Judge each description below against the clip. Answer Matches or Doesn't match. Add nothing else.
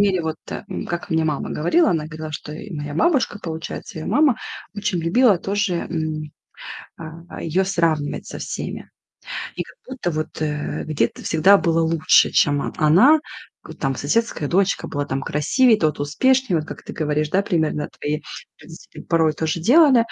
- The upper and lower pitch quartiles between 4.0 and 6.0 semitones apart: Matches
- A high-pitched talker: Doesn't match